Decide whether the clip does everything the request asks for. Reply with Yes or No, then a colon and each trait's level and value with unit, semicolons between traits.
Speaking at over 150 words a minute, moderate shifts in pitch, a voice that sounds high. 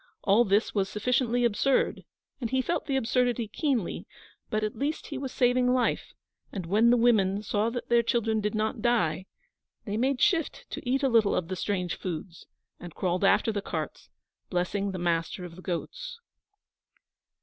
Yes: average, 175 wpm; average, 4.3 semitones; high, 220 Hz